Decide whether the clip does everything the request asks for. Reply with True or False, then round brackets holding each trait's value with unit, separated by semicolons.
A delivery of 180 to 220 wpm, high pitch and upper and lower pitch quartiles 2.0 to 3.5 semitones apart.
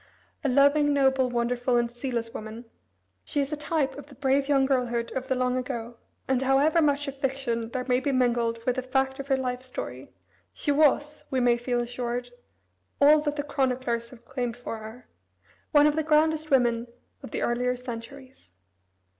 True (185 wpm; 260 Hz; 2.6 semitones)